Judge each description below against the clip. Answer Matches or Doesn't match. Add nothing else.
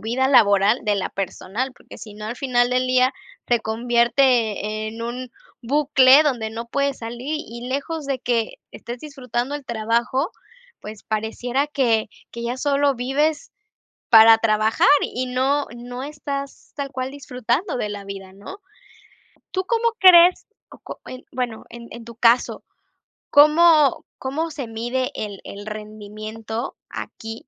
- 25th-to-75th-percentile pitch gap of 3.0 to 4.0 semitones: Matches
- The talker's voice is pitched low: Doesn't match